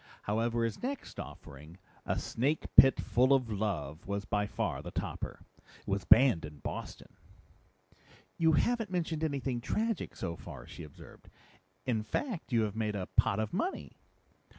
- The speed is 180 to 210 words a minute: No, average, 155 wpm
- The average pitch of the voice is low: Yes, low, 115 Hz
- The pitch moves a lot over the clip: Yes, wide, 7.2 semitones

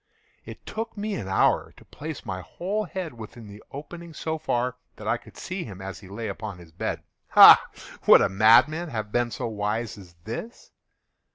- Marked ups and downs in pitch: Yes, wide, 7.8 semitones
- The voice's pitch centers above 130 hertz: No, low, 115 Hz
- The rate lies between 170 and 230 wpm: Yes, average, 185 wpm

